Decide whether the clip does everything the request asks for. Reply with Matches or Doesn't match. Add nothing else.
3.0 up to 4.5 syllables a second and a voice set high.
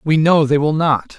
Doesn't match